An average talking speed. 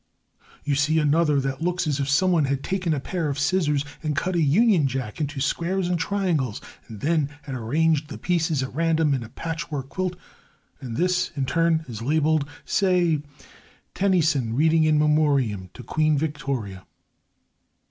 Yes: average, 165 wpm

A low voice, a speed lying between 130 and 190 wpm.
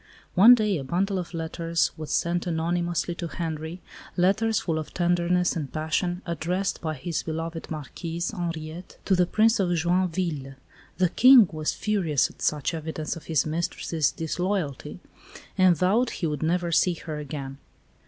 No: medium, 170 Hz; average, 155 wpm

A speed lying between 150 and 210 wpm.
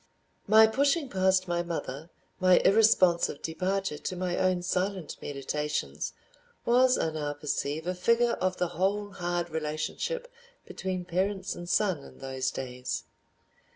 No: slow, 135 wpm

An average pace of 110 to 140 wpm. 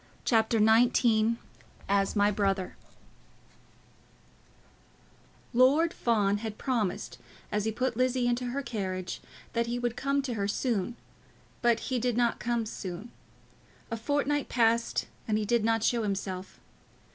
Yes: slow, 135 wpm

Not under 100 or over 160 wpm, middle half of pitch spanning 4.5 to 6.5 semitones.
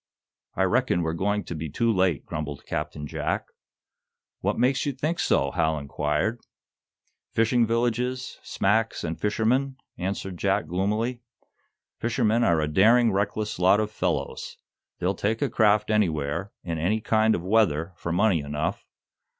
Yes: average, 145 wpm; average, 5.1 semitones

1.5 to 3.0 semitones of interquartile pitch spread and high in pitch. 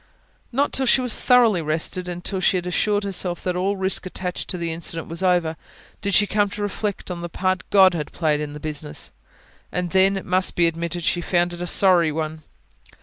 No: narrow, 2.6 semitones; medium, 180 Hz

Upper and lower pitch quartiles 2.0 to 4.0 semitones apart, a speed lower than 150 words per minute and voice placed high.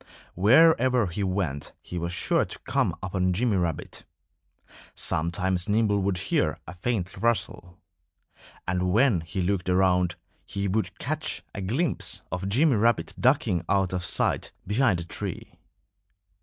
No: average, 3.7 semitones; average, 140 wpm; very low, 95 Hz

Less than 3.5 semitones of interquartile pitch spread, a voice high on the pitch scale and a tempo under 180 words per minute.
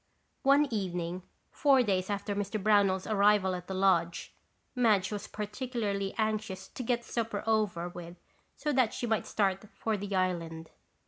Yes: average, 2.9 semitones; high, 205 Hz; average, 150 wpm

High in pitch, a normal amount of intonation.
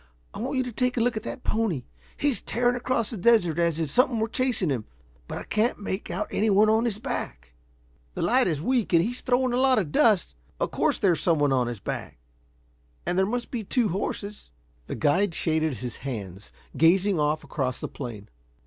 No: high, 200 Hz; wide, 7.7 semitones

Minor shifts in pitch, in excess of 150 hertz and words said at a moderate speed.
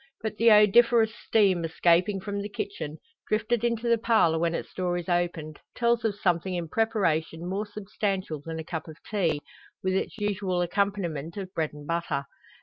No: average, 4.2 semitones; high, 190 Hz; average, 175 wpm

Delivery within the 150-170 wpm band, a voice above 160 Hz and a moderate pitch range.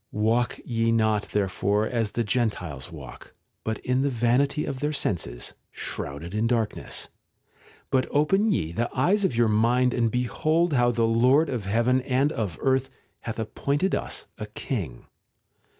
No: average, 160 wpm; low, 120 Hz; average, 3.8 semitones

